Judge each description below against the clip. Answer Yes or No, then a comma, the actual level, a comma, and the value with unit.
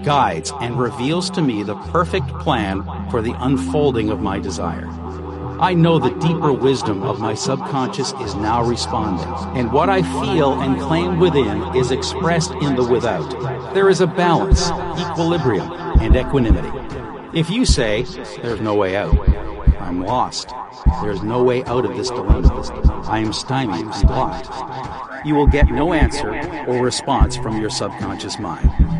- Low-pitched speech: Yes, low, 125 Hz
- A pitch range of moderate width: No, wide, 8.3 semitones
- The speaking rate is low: No, average, 160 wpm